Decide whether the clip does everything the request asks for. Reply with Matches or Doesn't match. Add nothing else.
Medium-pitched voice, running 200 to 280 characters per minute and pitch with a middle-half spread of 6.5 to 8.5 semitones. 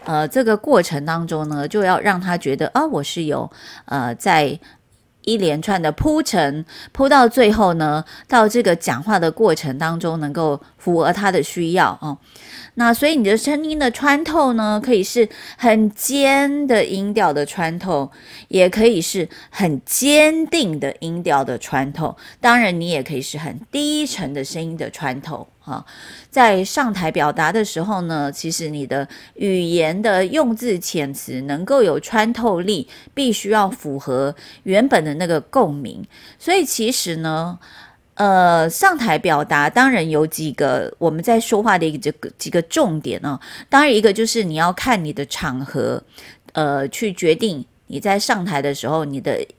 Matches